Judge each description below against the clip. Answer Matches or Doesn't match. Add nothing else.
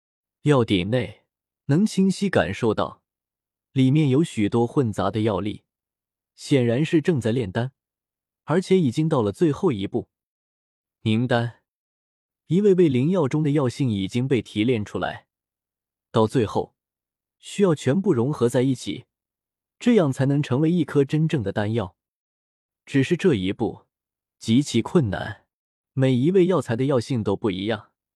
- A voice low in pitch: Matches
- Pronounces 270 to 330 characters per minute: Doesn't match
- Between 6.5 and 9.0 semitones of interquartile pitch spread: Matches